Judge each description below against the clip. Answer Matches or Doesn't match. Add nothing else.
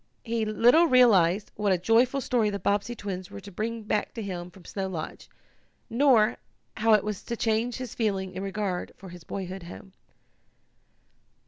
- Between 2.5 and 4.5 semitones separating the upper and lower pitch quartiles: Matches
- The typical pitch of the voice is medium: Doesn't match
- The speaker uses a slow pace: Doesn't match